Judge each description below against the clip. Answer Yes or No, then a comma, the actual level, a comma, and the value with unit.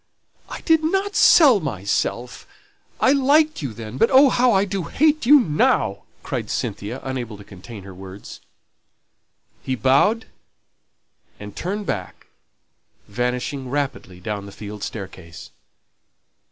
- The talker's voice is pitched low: Yes, low, 130 Hz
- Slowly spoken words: Yes, slow, 125 wpm